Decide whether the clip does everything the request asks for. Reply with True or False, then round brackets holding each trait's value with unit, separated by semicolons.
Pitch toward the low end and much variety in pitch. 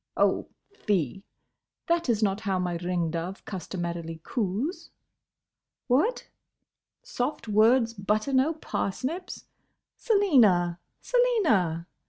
False (215 Hz; 8.7 semitones)